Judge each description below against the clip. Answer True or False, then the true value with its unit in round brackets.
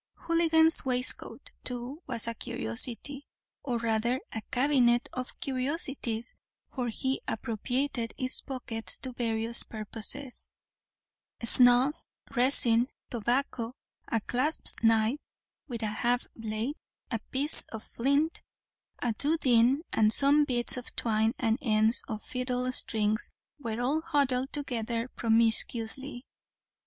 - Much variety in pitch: False (2.9 semitones)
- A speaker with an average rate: False (115 wpm)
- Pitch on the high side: True (245 Hz)